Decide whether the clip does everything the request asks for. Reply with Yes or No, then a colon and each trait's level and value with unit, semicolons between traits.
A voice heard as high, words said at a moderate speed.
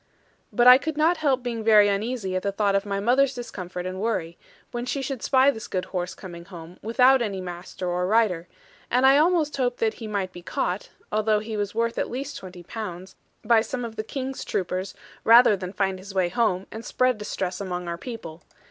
No: high, 210 Hz; fast, 210 wpm